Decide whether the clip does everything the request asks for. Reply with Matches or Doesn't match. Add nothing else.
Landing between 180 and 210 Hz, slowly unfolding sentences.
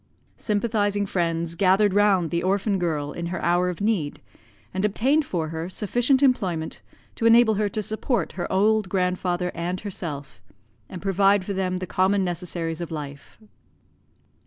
Doesn't match